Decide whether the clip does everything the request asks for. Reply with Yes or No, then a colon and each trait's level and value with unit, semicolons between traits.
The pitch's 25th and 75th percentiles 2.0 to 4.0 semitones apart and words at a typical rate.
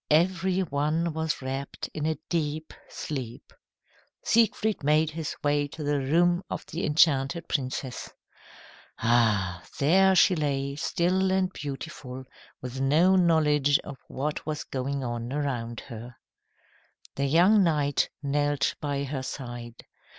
No: average, 3.7 semitones; slow, 130 wpm